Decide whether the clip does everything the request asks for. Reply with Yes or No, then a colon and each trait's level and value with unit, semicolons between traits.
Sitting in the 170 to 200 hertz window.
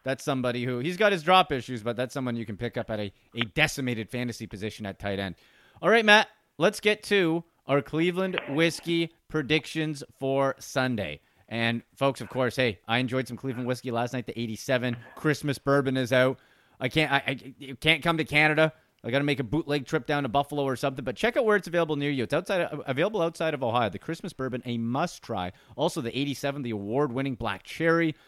No: low, 135 Hz